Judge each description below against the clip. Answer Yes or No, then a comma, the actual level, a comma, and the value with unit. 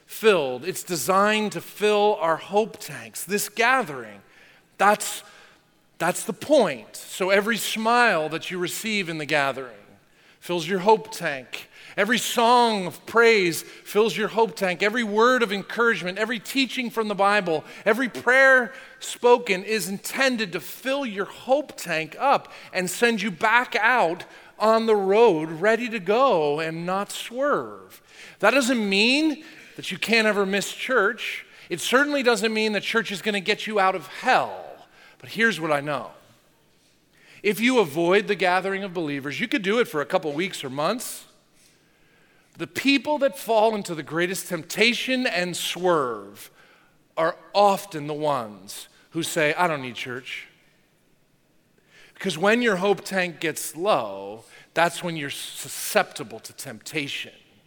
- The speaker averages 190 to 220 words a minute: No, average, 155 wpm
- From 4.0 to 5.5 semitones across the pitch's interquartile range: Yes, average, 4.8 semitones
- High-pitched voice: Yes, high, 200 Hz